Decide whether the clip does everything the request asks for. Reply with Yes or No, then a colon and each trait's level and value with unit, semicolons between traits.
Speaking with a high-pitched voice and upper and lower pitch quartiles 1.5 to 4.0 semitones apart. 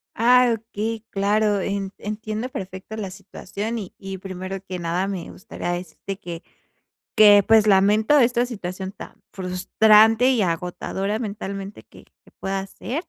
Yes: high, 200 Hz; narrow, 2.5 semitones